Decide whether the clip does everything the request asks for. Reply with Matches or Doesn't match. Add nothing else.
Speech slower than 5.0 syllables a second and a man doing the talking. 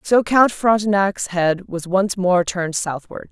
Doesn't match